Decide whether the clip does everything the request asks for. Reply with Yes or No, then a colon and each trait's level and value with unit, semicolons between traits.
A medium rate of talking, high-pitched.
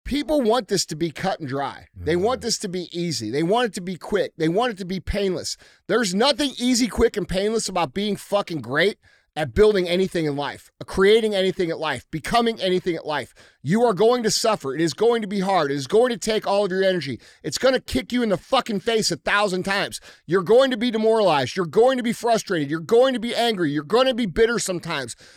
No: fast, 240 wpm; high, 195 Hz